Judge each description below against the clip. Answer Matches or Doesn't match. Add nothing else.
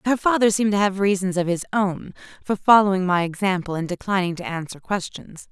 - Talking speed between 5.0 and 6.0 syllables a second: Matches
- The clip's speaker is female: Matches